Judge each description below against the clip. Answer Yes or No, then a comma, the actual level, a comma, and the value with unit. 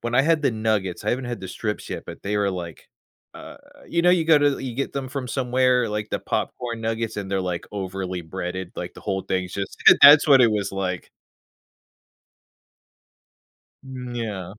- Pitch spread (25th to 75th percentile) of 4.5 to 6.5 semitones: Yes, average, 5.2 semitones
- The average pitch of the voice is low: Yes, low, 110 Hz